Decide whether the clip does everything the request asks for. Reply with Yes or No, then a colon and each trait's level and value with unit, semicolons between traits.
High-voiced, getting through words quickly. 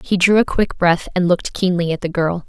No: medium, 180 Hz; fast, 265 wpm